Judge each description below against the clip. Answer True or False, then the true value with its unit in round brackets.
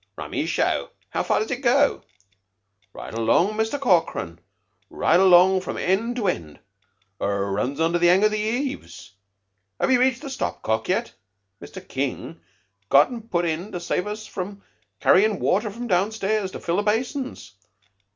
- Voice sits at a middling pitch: False (195 Hz)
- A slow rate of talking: False (160 wpm)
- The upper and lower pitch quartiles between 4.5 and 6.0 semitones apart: True (5.2 semitones)